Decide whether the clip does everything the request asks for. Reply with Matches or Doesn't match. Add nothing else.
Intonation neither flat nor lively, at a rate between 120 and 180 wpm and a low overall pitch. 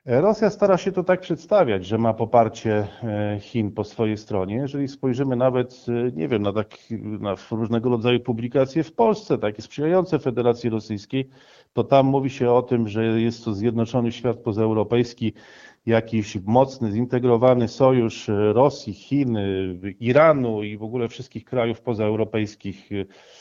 Matches